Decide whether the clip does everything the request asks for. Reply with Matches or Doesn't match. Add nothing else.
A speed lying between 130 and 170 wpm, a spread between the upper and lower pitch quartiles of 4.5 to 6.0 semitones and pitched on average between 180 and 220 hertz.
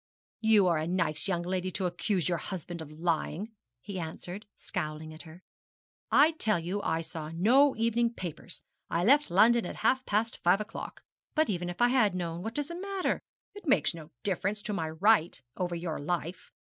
Doesn't match